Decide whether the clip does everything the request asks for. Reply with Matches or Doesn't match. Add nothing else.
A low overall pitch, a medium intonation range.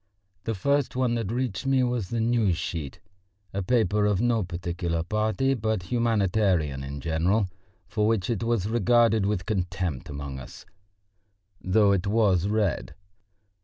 Matches